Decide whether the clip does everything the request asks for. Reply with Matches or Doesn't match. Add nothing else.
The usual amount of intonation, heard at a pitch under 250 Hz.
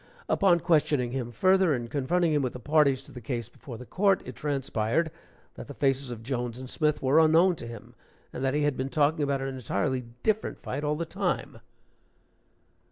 Matches